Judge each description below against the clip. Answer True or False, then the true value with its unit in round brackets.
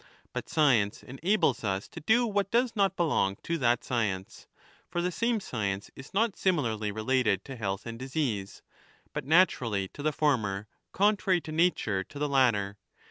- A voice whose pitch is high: False (130 Hz)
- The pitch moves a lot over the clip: True (9.0 semitones)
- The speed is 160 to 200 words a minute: True (165 wpm)